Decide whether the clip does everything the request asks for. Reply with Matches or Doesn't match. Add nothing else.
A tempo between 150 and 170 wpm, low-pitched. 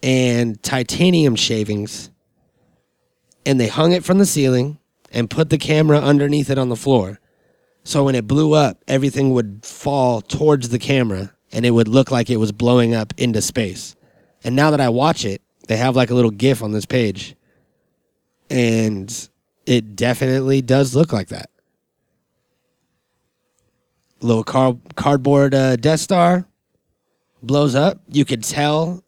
Matches